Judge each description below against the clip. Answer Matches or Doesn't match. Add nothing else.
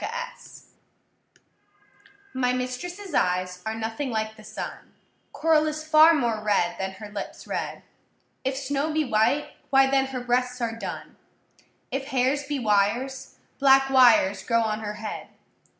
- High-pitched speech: Matches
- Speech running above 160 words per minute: Doesn't match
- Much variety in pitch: Doesn't match